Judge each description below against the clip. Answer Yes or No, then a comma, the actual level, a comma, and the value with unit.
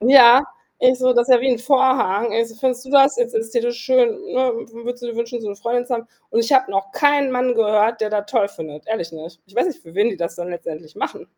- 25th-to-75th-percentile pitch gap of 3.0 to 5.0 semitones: Yes, average, 3.6 semitones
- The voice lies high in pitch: Yes, high, 235 Hz